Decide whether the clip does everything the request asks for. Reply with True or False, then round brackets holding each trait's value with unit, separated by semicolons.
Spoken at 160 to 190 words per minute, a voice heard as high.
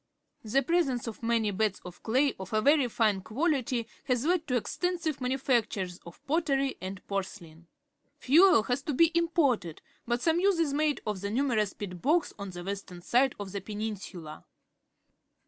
True (175 wpm; 240 Hz)